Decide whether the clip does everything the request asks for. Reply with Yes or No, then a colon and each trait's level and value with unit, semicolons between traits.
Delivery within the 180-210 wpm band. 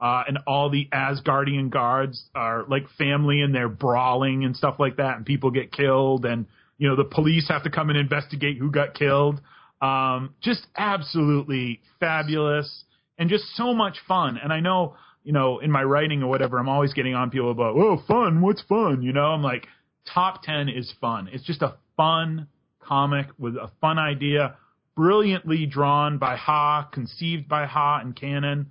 Yes: average, 185 wpm